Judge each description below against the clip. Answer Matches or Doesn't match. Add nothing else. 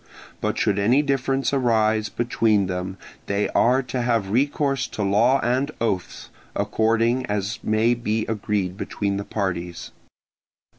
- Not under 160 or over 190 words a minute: Doesn't match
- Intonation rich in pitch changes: Doesn't match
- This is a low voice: Matches